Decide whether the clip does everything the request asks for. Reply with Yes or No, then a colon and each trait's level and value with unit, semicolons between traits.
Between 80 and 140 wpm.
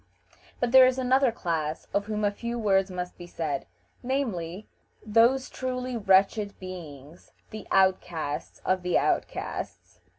Yes: slow, 135 wpm